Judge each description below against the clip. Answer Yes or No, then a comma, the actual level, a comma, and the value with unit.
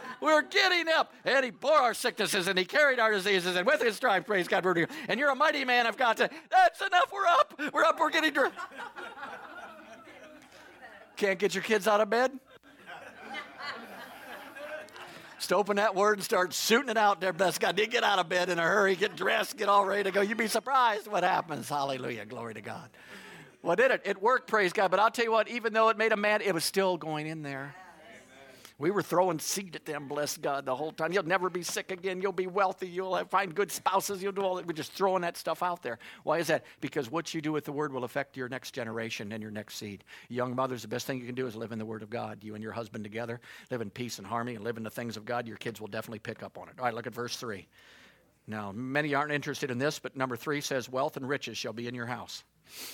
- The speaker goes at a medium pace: No, fast, 250 wpm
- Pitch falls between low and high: Yes, medium, 180 Hz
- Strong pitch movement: Yes, wide, 9.0 semitones